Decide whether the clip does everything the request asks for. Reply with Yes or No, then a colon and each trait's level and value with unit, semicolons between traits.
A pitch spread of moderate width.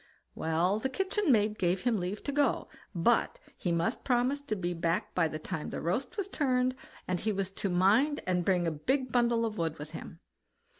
No: wide, 6.5 semitones